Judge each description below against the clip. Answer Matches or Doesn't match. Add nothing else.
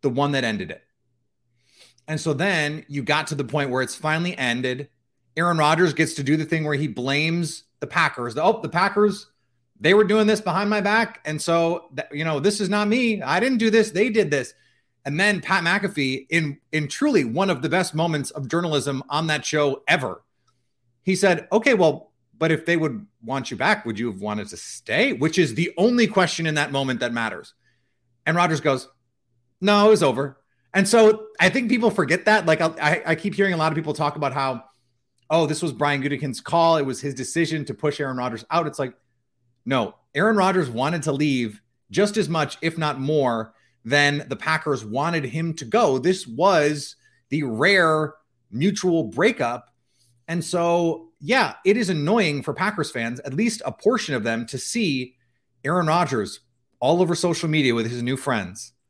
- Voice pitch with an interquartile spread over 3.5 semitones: Matches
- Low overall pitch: Doesn't match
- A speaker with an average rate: Matches